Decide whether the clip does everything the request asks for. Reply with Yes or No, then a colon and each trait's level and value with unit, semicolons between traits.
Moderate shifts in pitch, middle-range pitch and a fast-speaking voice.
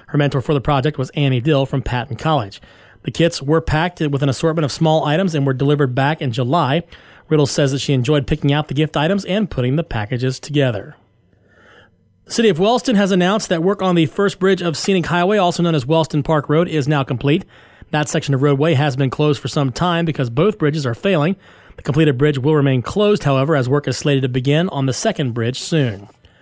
Yes: average, 3.5 semitones; medium, 150 Hz; fast, 225 wpm